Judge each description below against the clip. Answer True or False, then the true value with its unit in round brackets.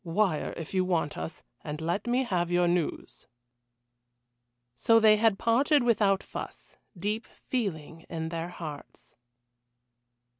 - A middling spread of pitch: True (5.0 semitones)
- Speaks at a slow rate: True (125 wpm)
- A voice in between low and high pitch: True (180 Hz)